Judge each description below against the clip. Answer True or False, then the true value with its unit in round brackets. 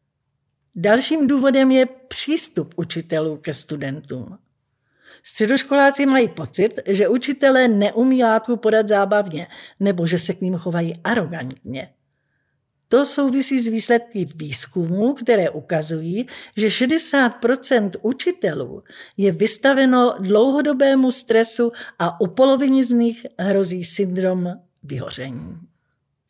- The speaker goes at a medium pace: False (105 wpm)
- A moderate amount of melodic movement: False (7.5 semitones)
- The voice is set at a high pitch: True (210 Hz)